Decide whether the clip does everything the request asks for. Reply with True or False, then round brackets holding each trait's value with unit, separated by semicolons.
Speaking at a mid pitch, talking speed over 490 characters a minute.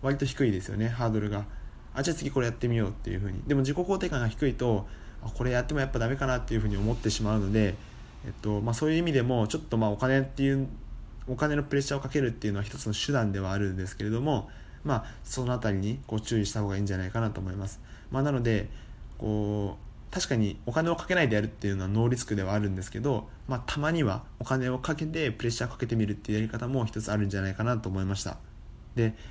False (115 Hz; 520 characters per minute)